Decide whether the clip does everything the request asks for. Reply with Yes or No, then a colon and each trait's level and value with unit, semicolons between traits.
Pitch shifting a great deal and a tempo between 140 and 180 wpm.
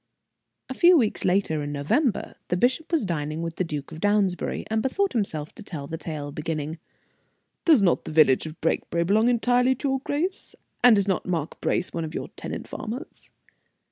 No: wide, 7.7 semitones; average, 190 wpm